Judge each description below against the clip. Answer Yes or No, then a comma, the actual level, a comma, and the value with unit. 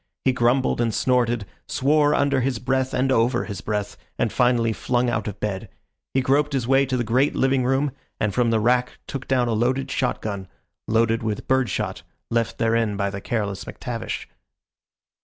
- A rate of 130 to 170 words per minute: No, average, 185 wpm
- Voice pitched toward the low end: Yes, low, 120 Hz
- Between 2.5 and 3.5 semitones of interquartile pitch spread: Yes, average, 2.8 semitones